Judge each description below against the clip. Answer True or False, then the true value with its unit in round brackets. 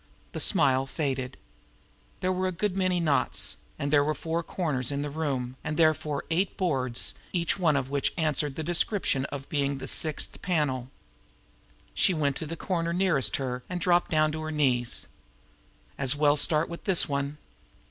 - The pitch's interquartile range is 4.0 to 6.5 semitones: False (3.6 semitones)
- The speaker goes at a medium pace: True (180 wpm)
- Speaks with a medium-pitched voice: True (150 Hz)